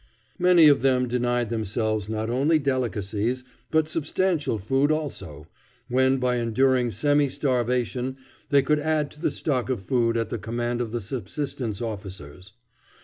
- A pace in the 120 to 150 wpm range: Yes, average, 145 wpm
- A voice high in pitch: No, low, 125 Hz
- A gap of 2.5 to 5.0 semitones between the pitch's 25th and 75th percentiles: Yes, average, 3.9 semitones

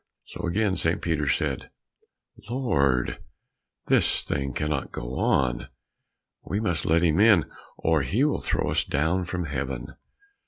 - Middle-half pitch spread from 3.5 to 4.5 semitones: No, average, 5.3 semitones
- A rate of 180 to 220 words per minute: No, average, 140 wpm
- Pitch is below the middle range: Yes, very low, 80 Hz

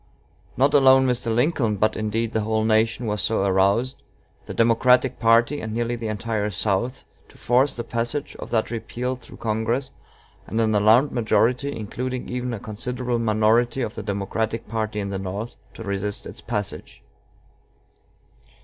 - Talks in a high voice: No, low, 115 Hz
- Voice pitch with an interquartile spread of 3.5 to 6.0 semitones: No, narrow, 2.5 semitones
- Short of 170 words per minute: Yes, average, 160 wpm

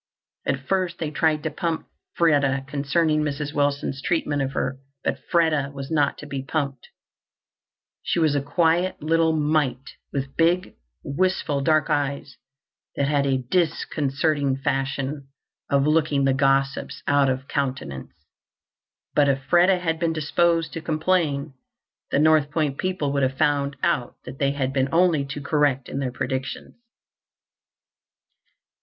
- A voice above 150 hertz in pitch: No, medium, 145 Hz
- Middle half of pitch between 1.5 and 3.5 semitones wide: Yes, average, 2.7 semitones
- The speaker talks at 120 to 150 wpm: Yes, average, 145 wpm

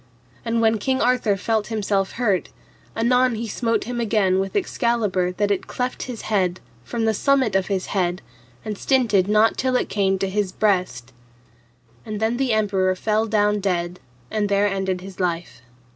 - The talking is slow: No, average, 175 wpm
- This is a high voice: Yes, high, 210 Hz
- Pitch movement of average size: Yes, average, 3.2 semitones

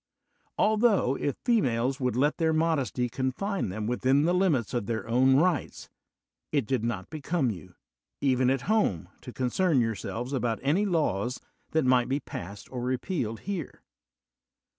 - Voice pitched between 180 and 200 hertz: No, low, 130 Hz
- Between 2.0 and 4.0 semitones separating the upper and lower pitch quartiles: No, average, 5.1 semitones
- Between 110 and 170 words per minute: Yes, average, 150 wpm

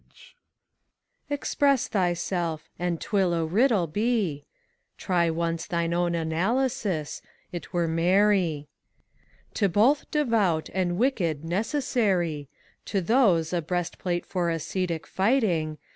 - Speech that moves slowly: Yes, slow, 125 wpm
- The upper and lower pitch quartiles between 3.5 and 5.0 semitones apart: Yes, average, 4.1 semitones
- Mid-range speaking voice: Yes, medium, 175 Hz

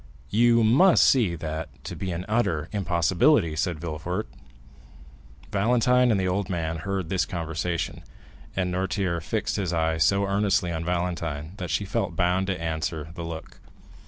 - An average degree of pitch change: Yes, average, 3.4 semitones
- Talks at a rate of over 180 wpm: No, average, 160 wpm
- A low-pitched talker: Yes, very low, 90 Hz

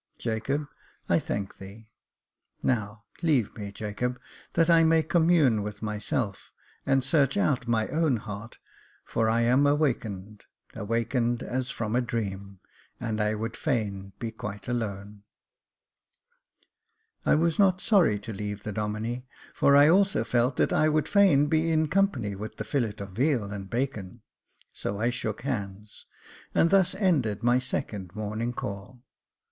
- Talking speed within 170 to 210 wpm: No, average, 150 wpm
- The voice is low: Yes, low, 115 Hz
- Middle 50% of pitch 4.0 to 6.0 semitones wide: Yes, wide, 5.5 semitones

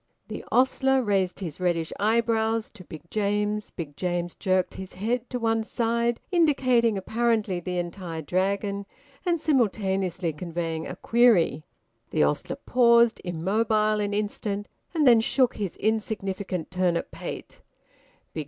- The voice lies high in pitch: Yes, high, 205 Hz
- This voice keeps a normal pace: No, slow, 130 wpm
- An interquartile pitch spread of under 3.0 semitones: No, average, 4.2 semitones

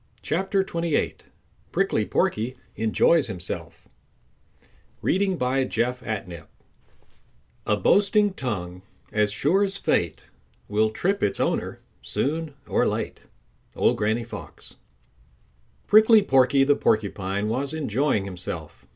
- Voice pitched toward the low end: Yes, low, 125 Hz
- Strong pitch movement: Yes, wide, 8.1 semitones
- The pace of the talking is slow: Yes, slow, 95 wpm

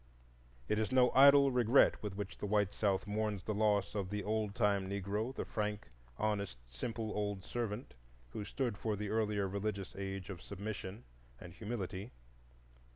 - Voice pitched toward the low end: Yes, low, 105 Hz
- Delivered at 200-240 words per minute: No, average, 160 wpm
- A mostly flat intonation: Yes, narrow, 1.7 semitones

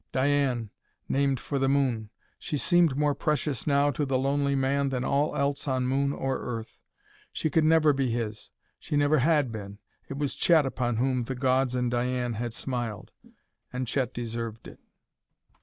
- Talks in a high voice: No, low, 135 Hz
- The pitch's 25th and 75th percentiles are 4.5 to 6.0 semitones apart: No, average, 2.7 semitones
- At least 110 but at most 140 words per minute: No, average, 175 wpm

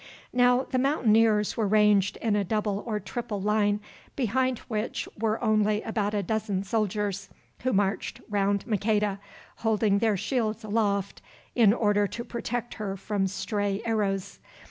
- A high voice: Yes, high, 210 Hz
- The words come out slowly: No, average, 145 wpm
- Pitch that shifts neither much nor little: No, narrow, 1.9 semitones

